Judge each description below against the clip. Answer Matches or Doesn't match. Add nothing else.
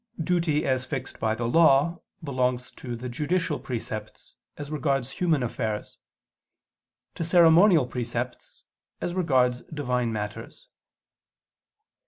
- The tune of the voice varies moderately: Matches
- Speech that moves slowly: Matches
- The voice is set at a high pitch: Doesn't match